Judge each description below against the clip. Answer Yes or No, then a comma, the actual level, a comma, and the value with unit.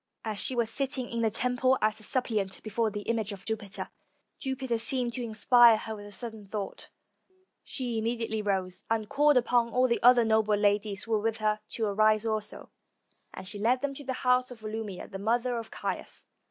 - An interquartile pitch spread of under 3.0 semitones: Yes, narrow, 2.6 semitones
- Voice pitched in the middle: No, high, 225 Hz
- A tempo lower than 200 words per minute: No, fast, 205 wpm